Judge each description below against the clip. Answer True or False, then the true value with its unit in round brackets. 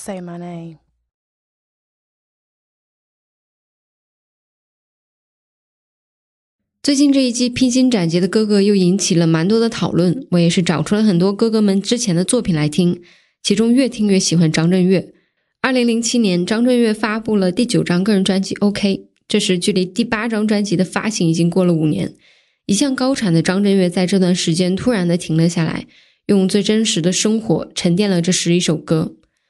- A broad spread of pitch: False (4.0 semitones)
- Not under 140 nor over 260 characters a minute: True (250 characters per minute)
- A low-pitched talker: False (190 Hz)